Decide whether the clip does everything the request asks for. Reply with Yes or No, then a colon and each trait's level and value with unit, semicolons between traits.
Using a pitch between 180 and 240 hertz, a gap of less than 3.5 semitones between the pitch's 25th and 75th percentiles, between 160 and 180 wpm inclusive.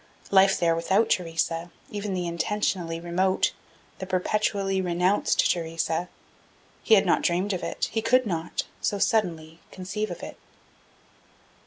No: medium, 185 Hz; average, 3.0 semitones; slow, 135 wpm